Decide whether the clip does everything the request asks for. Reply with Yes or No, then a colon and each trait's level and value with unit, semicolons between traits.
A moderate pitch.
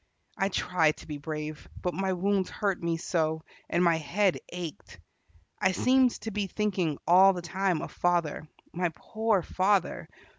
Yes: medium, 180 Hz